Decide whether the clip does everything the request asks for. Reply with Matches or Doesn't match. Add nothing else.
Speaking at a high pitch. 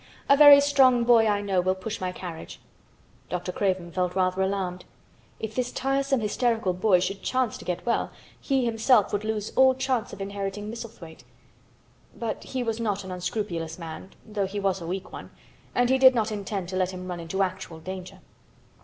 Matches